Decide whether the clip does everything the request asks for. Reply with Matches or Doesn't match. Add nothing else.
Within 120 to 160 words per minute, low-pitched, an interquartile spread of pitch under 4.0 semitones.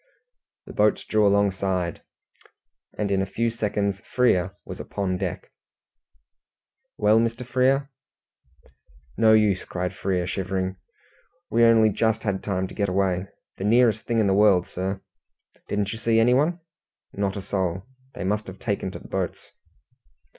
Matches